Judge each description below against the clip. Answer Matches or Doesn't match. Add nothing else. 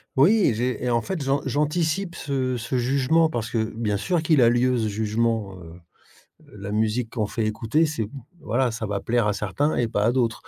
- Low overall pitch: Matches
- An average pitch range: Matches